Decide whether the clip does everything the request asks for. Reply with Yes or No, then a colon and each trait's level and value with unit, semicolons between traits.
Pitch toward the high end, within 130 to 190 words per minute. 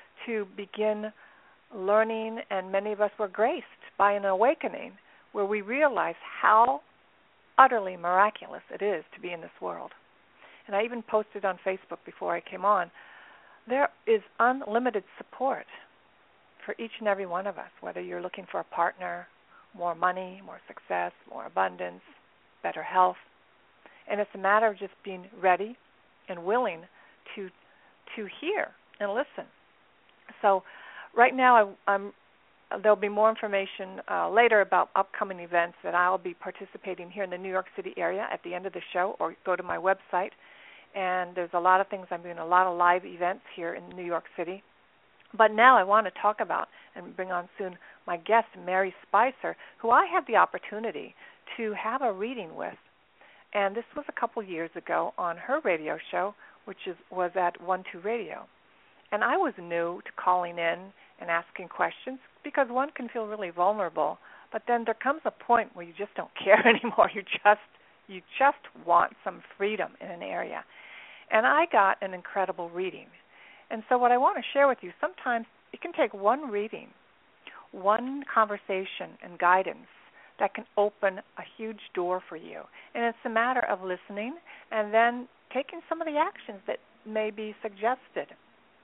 Yes: high, 205 Hz; average, 175 wpm